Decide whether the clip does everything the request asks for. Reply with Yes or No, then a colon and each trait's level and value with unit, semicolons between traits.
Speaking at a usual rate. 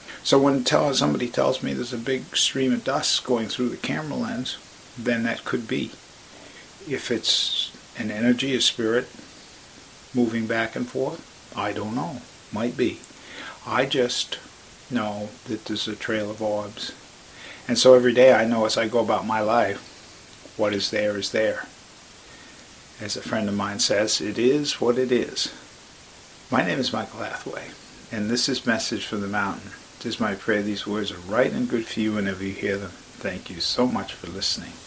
Yes: average, 180 wpm